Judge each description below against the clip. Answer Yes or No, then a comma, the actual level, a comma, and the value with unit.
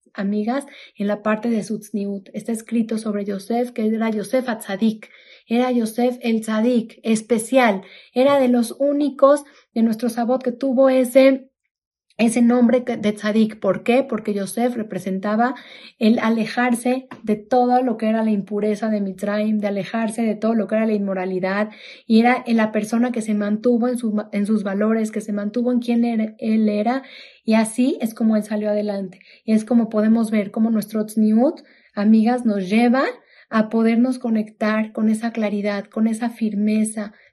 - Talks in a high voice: Yes, high, 225 Hz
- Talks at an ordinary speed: Yes, average, 170 wpm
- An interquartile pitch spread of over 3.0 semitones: No, narrow, 2.5 semitones